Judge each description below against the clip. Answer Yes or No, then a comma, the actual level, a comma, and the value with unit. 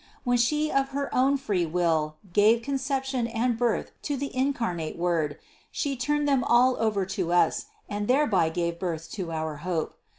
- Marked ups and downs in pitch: Yes, wide, 7.5 semitones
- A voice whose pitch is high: Yes, high, 225 Hz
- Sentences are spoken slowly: No, average, 170 wpm